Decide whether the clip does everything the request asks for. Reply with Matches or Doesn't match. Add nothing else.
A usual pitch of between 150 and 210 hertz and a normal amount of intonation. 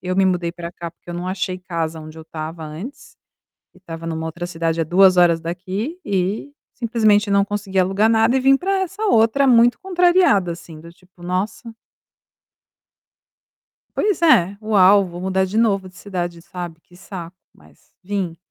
Matches